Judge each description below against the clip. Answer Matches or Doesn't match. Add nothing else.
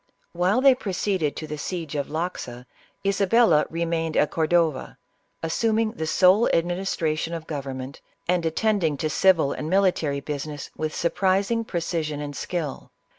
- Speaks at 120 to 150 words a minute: Matches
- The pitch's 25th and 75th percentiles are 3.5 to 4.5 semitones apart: Matches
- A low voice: Doesn't match